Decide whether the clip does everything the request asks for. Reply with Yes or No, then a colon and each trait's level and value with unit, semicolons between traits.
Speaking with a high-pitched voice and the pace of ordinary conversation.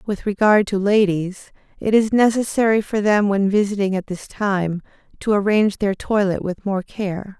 Yes: high, 200 Hz; average, 170 wpm